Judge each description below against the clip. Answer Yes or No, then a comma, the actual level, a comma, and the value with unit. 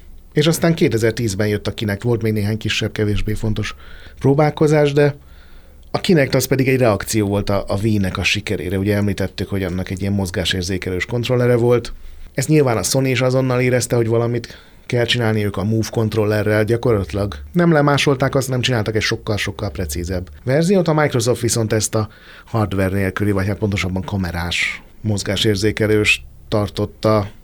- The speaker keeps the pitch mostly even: No, average, 3.7 semitones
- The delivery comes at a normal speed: No, fast, 160 wpm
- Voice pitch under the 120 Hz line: Yes, low, 110 Hz